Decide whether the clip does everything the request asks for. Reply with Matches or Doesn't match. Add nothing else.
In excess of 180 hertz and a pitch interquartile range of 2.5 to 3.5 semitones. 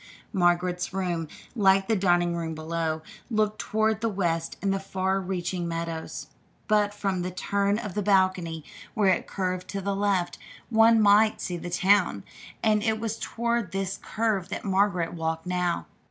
Matches